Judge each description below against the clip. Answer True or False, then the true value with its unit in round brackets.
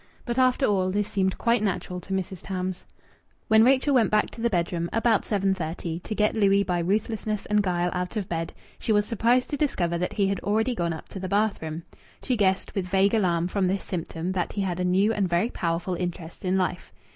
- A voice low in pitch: False (195 Hz)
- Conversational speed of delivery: False (215 wpm)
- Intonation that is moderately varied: True (3.2 semitones)